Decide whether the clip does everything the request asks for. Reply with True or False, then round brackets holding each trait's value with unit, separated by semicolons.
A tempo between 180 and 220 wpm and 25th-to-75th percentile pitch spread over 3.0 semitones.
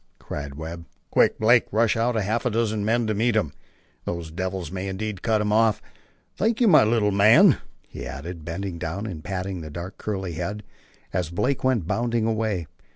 True (185 wpm; 4.5 semitones)